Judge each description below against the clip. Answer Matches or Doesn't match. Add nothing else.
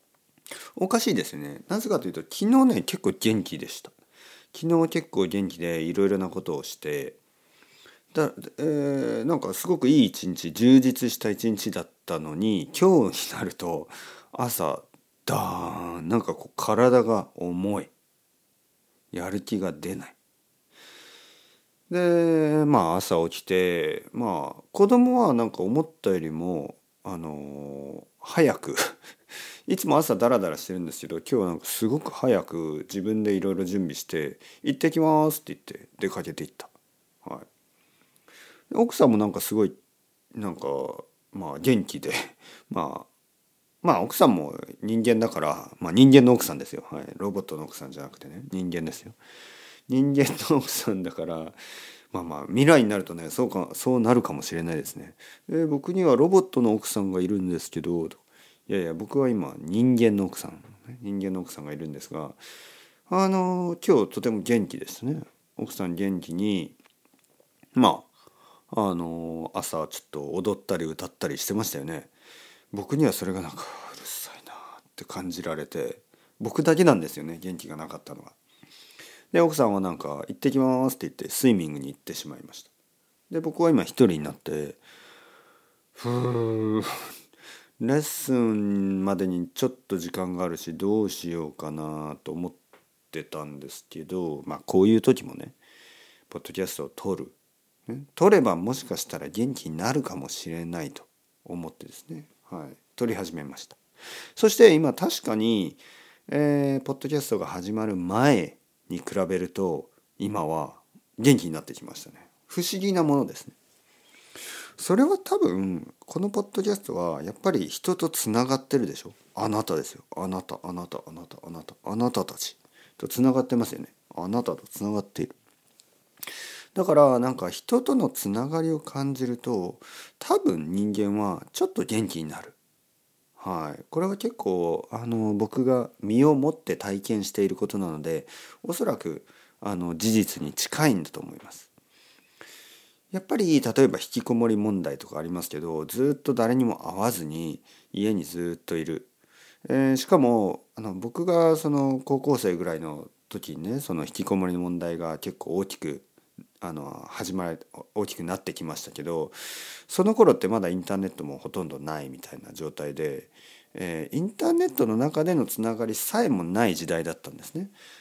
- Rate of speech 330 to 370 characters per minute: Doesn't match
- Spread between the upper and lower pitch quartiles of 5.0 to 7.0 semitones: Doesn't match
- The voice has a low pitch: Matches